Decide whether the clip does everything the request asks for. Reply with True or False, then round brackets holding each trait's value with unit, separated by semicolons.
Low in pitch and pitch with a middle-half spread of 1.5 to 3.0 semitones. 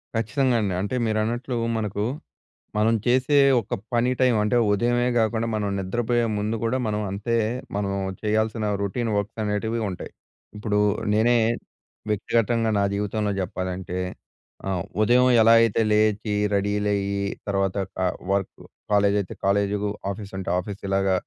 True (105 Hz; 2.4 semitones)